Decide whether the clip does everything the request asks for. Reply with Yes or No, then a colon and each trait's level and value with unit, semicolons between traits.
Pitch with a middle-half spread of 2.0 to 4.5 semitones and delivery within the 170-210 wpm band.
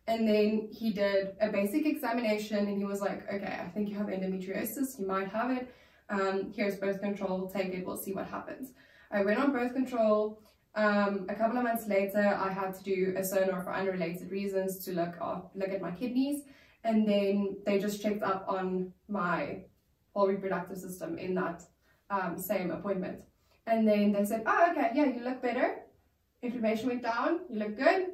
Yes: average, 2.8 semitones; average, 190 wpm